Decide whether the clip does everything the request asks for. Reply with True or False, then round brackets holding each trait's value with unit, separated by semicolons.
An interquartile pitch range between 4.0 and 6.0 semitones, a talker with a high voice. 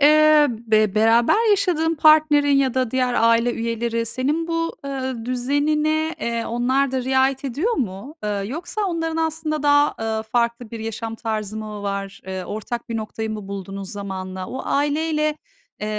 True (5.5 semitones; 250 Hz)